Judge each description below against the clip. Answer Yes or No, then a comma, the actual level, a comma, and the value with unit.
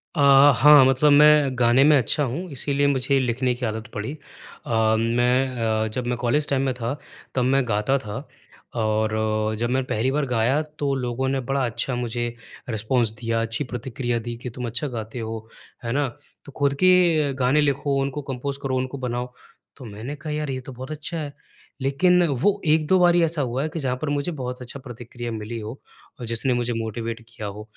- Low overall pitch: Yes, low, 125 Hz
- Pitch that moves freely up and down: No, average, 3.2 semitones